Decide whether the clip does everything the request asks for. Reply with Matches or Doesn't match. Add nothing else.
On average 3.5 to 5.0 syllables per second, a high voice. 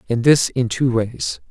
Doesn't match